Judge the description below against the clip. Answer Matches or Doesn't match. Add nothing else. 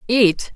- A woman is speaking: Matches